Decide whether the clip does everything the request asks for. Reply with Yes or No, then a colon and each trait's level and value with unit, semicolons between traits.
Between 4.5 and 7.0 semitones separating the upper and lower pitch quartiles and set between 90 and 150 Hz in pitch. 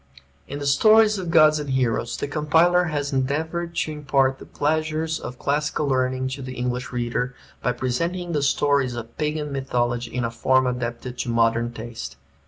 No: average, 3.8 semitones; low, 135 Hz